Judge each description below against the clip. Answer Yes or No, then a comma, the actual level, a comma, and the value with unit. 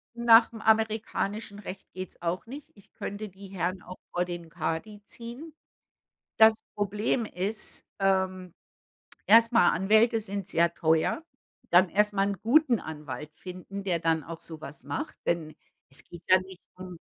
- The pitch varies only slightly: No, average, 3.9 semitones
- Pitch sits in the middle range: No, high, 195 Hz